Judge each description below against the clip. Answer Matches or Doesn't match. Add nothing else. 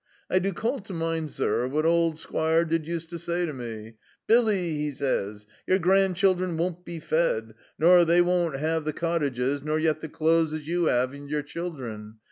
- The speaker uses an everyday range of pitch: Matches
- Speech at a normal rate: Matches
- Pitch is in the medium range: Matches